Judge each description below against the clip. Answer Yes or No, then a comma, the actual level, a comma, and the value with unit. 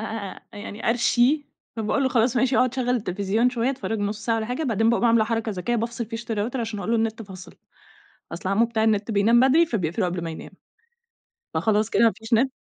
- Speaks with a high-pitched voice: Yes, high, 225 Hz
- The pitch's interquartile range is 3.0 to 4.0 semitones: No, narrow, 2.4 semitones